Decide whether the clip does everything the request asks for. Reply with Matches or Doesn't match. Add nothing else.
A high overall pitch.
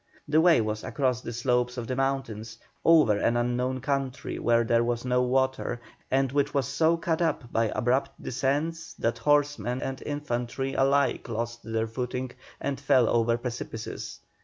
Doesn't match